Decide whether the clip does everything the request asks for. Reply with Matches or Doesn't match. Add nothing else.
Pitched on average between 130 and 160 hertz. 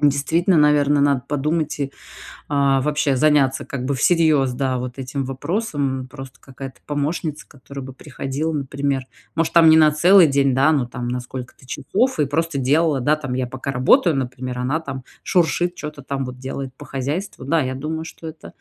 Matches